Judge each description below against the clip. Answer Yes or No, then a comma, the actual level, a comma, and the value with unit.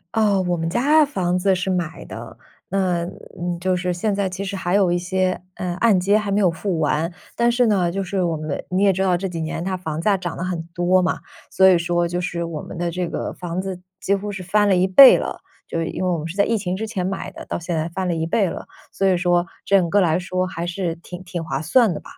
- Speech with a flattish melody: Yes, narrow, 2.2 semitones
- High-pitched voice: No, medium, 180 Hz